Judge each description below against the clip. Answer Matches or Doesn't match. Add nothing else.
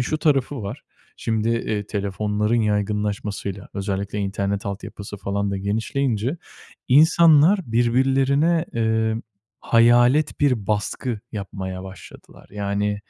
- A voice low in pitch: Matches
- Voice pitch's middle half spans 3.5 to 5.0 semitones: Matches